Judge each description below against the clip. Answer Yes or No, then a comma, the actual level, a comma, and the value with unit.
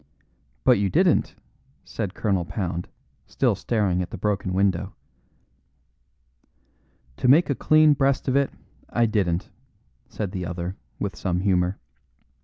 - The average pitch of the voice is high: No, low, 100 Hz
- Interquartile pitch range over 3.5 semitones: Yes, average, 4.2 semitones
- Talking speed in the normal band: No, slow, 130 wpm